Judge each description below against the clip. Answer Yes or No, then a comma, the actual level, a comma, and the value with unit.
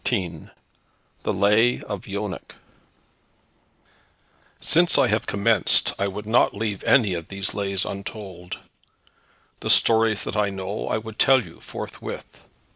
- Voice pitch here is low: Yes, low, 100 Hz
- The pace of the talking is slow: Yes, slow, 130 wpm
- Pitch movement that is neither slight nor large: No, narrow, 2.3 semitones